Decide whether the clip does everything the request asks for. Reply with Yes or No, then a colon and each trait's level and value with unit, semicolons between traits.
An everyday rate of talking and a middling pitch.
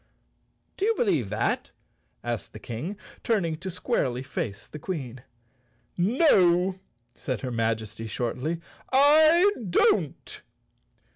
No: slow, 110 wpm; medium, 165 Hz